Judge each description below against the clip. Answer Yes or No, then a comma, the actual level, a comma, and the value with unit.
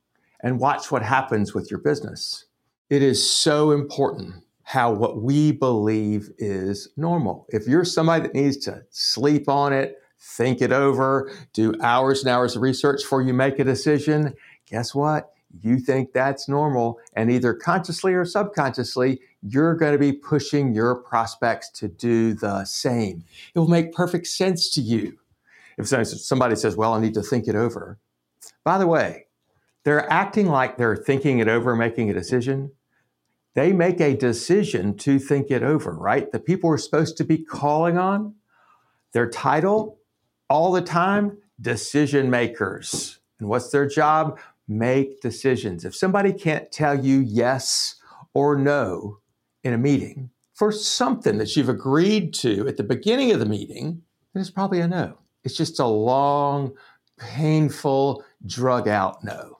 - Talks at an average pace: Yes, average, 160 wpm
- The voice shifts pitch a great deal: No, average, 4.6 semitones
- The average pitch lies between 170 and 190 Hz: No, low, 135 Hz